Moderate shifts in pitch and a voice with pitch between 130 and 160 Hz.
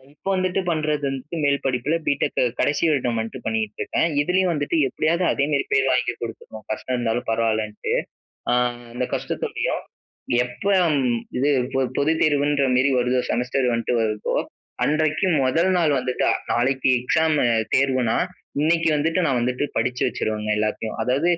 Yes: average, 4.1 semitones; low, 135 Hz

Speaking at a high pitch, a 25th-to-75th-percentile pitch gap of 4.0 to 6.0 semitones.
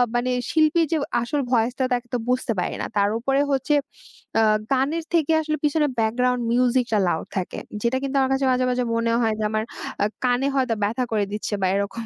No: very high, 250 Hz; average, 3.2 semitones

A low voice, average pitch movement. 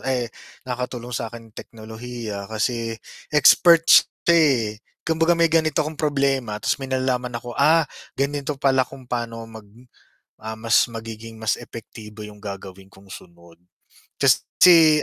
Yes: low, 120 Hz; average, 4.0 semitones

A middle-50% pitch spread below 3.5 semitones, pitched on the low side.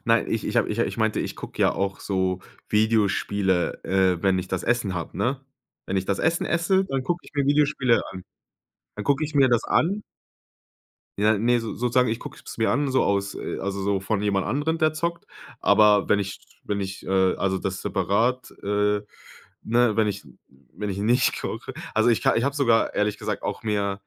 No: average, 4.4 semitones; low, 105 Hz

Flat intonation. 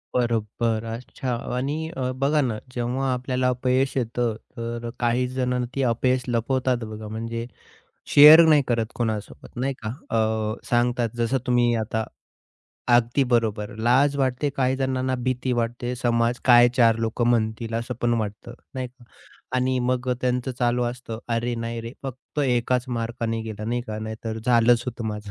Yes: narrow, 1.7 semitones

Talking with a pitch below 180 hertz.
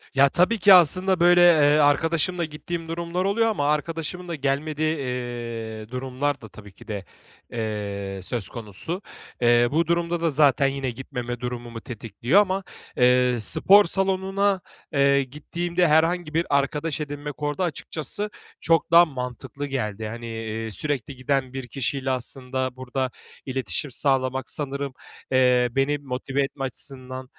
Yes: medium, 140 Hz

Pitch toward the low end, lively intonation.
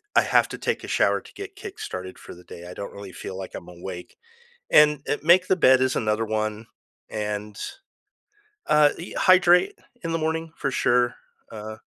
Yes: low, 125 Hz; wide, 7.9 semitones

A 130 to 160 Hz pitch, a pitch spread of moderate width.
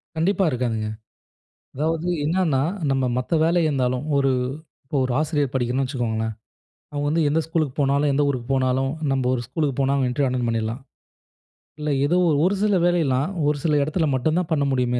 Yes: medium, 140 Hz; average, 3.7 semitones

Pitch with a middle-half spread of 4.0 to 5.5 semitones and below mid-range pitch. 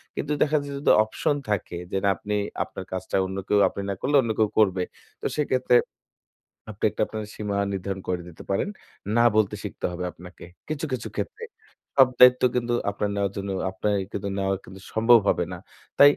Yes: average, 4.7 semitones; low, 105 Hz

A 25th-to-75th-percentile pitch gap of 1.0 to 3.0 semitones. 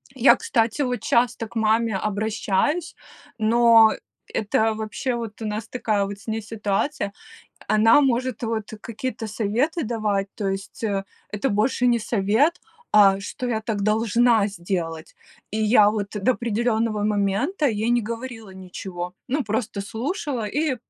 Yes: average, 2.7 semitones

